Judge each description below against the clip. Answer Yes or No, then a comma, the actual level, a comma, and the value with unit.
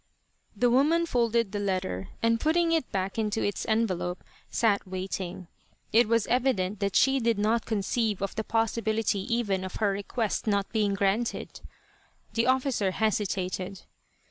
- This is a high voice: Yes, high, 215 Hz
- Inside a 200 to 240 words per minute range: No, average, 145 wpm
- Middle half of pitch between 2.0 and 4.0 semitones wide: Yes, average, 3.1 semitones